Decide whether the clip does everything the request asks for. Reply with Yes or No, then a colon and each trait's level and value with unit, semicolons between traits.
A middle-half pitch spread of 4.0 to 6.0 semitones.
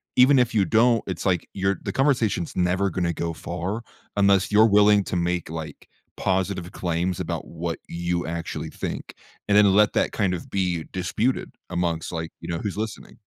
No: average, 3.2 semitones